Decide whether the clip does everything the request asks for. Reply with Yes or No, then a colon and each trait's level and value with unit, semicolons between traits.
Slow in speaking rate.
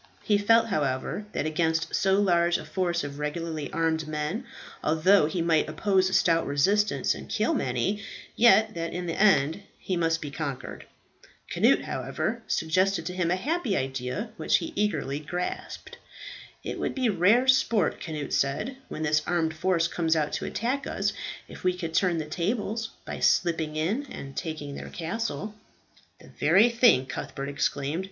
No: average, 165 wpm